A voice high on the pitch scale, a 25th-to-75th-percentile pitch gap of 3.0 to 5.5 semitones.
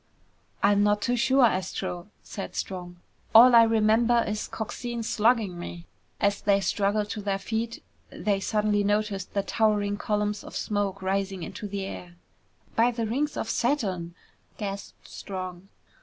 No: high, 205 Hz; narrow, 2.4 semitones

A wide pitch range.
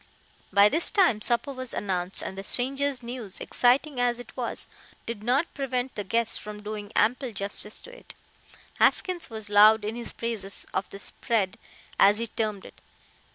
No: average, 3.5 semitones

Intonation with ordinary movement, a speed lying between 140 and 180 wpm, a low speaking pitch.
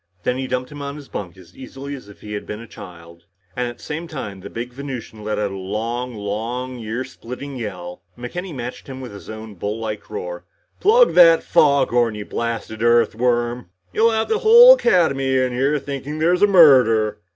No: average, 4.7 semitones; average, 195 wpm; low, 125 Hz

